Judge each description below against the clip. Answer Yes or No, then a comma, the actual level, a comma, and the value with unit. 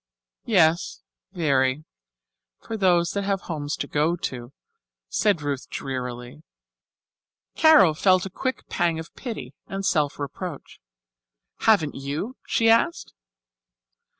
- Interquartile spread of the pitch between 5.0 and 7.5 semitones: Yes, wide, 5.5 semitones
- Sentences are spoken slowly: Yes, slow, 115 wpm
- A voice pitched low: No, medium, 165 Hz